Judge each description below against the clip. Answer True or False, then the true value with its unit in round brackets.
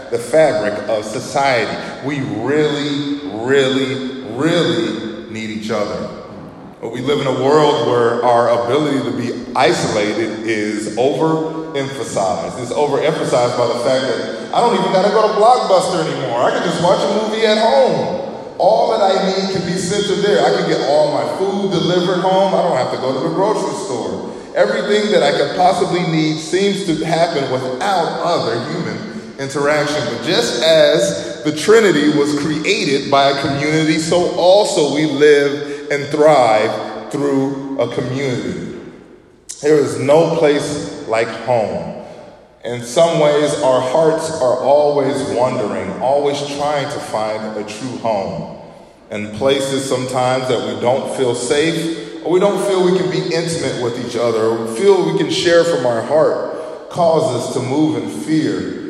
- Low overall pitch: False (145 Hz)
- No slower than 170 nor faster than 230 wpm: False (160 wpm)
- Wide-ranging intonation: False (4.5 semitones)